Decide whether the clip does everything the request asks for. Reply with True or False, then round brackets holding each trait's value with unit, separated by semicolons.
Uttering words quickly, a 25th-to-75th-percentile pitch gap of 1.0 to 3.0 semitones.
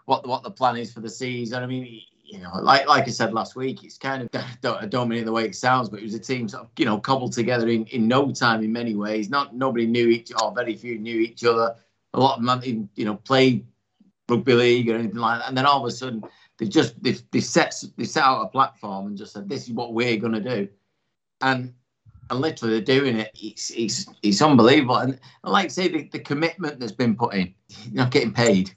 True (260 wpm; 2.6 semitones)